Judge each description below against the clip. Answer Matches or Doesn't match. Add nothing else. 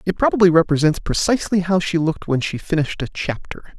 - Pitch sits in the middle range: Matches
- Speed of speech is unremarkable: Matches